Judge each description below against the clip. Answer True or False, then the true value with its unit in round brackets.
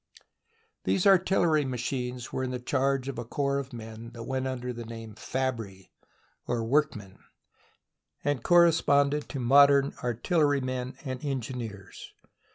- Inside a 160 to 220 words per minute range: False (135 wpm)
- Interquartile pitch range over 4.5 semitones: False (3.2 semitones)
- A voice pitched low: True (130 Hz)